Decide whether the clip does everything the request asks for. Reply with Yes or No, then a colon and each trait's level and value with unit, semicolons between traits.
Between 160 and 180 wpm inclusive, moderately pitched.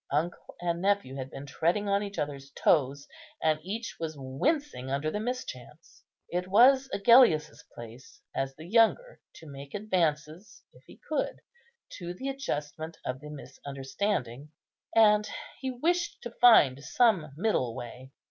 No: average, 145 wpm; medium, 165 Hz